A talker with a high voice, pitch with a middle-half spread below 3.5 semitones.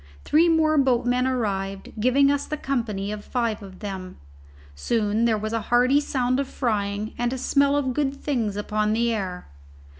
No: high, 235 Hz; average, 4.5 semitones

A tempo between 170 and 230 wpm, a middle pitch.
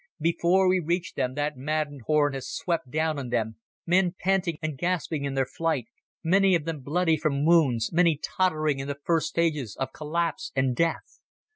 Yes: average, 180 wpm; medium, 155 Hz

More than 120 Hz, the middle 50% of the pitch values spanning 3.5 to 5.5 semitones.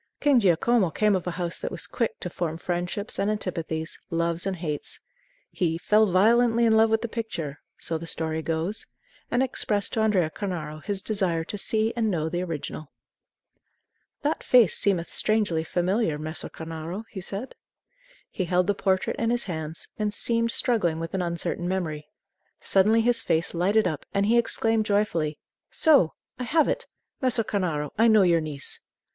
Yes: high, 190 Hz; average, 5.0 semitones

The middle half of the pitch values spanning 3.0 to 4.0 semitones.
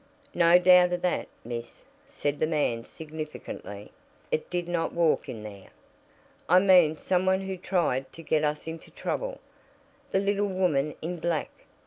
Yes: average, 3.3 semitones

